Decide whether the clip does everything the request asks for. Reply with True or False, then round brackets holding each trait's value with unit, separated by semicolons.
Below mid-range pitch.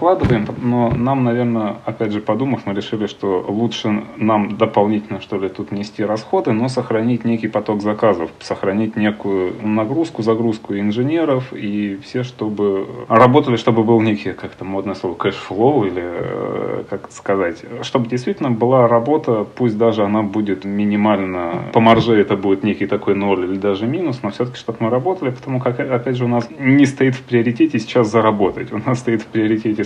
True (110 Hz)